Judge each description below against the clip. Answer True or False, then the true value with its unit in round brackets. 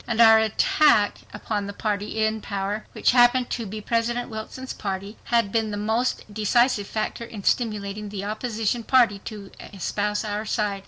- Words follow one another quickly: False (165 wpm)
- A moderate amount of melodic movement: False (2.1 semitones)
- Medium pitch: False (215 Hz)